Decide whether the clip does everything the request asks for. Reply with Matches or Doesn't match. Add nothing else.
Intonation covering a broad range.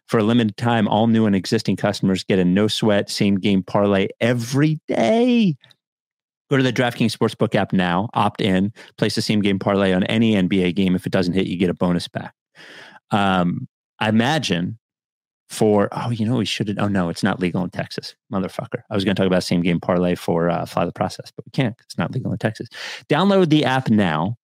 Doesn't match